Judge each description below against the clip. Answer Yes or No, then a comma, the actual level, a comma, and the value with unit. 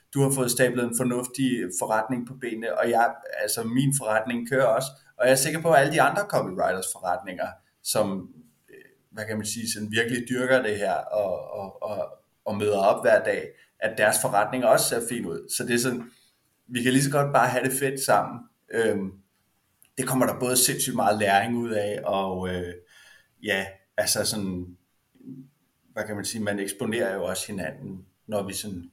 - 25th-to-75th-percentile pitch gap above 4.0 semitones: Yes, average, 4.5 semitones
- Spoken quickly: No, average, 190 wpm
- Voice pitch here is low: Yes, low, 115 Hz